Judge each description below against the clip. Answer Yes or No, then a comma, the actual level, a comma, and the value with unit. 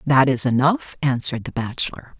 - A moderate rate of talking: Yes, average, 165 wpm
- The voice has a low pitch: Yes, low, 130 Hz